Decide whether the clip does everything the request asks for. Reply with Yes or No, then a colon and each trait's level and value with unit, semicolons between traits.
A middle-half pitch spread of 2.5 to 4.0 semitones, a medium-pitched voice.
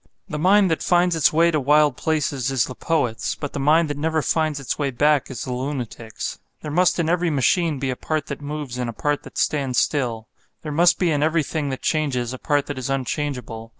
Yes: average, 3.3 semitones; medium, 145 Hz